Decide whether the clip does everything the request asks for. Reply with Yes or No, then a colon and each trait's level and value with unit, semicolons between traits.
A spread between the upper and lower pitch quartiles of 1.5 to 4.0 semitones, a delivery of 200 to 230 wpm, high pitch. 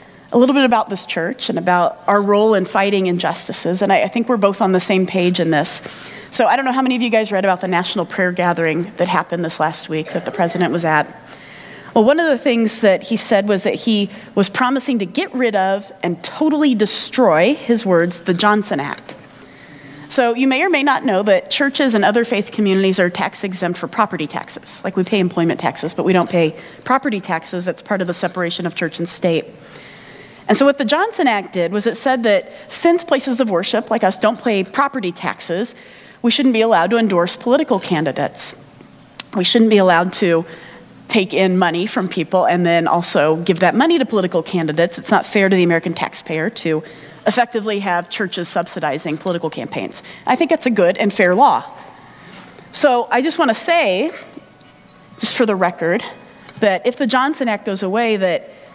No: wide, 5.5 semitones; fast, 205 wpm; high, 195 Hz